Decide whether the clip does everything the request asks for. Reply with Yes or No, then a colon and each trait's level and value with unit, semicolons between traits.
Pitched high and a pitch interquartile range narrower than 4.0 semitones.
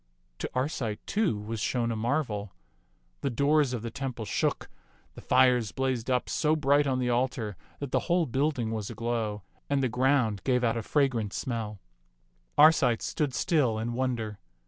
No: low, 125 Hz; average, 3.6 semitones